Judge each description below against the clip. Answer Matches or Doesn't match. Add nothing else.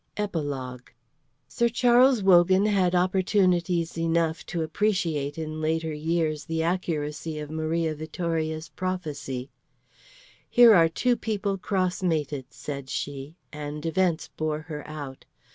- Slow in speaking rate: Matches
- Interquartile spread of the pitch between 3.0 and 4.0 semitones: Matches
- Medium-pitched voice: Matches